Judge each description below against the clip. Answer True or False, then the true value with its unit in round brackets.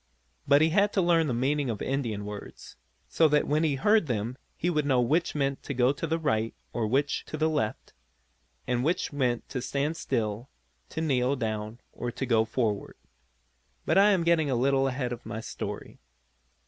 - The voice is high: False (135 Hz)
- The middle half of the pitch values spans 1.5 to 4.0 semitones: False (4.5 semitones)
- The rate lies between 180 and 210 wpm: True (190 wpm)